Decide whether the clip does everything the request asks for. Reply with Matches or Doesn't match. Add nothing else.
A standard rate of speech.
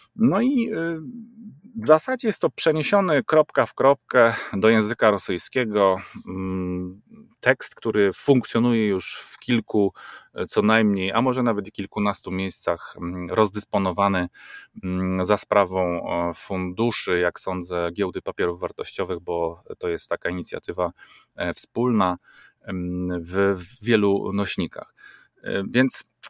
Doesn't match